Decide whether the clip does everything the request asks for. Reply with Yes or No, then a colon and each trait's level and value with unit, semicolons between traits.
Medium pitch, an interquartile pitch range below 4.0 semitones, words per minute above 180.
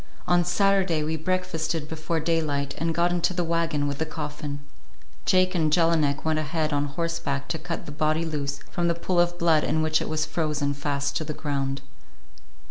Yes: medium, 160 Hz; narrow, 2.4 semitones; average, 190 wpm